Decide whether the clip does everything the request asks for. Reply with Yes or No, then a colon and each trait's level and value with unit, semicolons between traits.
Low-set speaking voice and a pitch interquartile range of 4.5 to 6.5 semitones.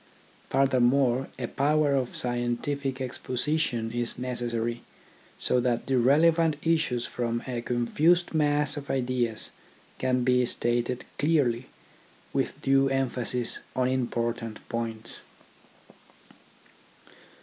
No: low, 125 Hz; narrow, 2.6 semitones